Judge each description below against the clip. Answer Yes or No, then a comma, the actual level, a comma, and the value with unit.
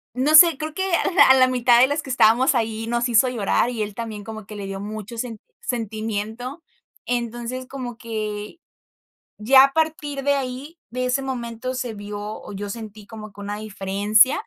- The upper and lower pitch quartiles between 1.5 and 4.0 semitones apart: Yes, average, 3.4 semitones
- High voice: Yes, high, 235 Hz